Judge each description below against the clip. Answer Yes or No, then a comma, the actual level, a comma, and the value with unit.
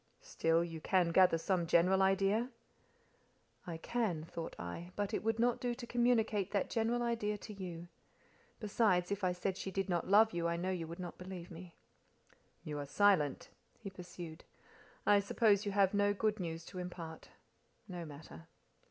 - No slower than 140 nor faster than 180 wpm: Yes, average, 175 wpm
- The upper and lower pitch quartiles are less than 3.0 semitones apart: No, average, 3.6 semitones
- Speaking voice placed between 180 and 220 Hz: Yes, high, 190 Hz